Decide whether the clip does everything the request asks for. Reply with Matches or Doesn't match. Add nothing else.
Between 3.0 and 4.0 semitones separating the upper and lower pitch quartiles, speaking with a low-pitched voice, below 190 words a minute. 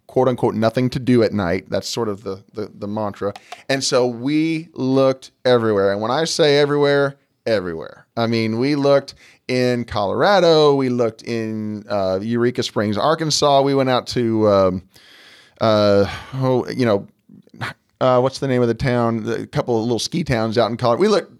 Matches